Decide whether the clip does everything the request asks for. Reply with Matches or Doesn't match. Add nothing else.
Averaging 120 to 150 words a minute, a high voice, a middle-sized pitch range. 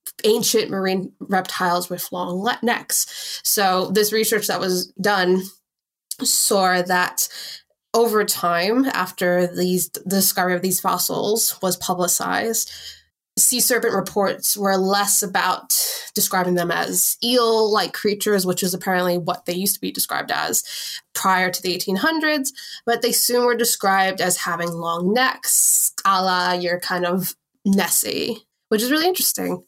Matches